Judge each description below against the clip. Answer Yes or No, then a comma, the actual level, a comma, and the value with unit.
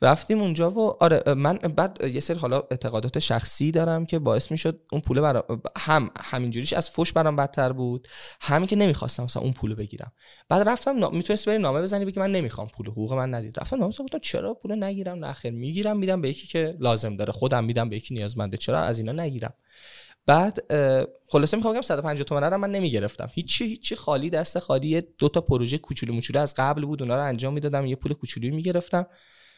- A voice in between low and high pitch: Yes, medium, 150 Hz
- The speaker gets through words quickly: Yes, fast, 205 wpm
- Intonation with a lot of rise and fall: Yes, wide, 5.8 semitones